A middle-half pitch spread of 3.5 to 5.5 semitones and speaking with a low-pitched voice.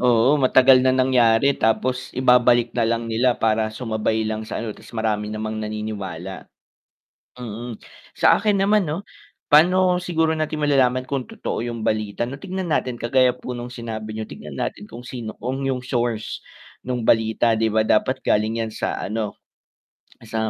No: average, 3.0 semitones; low, 120 Hz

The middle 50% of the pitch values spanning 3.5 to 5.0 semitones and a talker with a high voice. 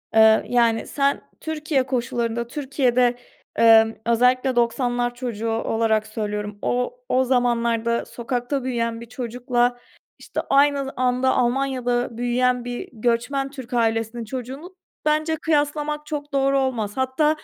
No: narrow, 2.6 semitones; high, 245 Hz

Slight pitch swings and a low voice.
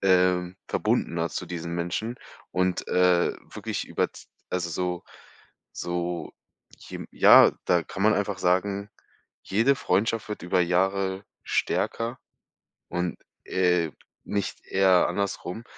Yes: narrow, 2.1 semitones; very low, 90 Hz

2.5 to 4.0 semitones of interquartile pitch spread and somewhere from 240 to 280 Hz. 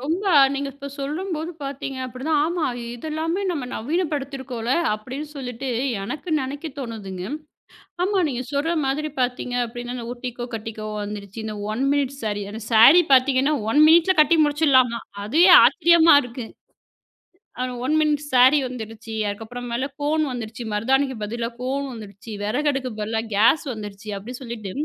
No: average, 4.5 semitones; very high, 255 Hz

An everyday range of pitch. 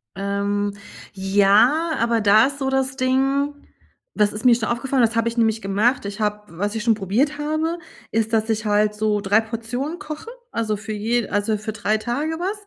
Yes: average, 4.2 semitones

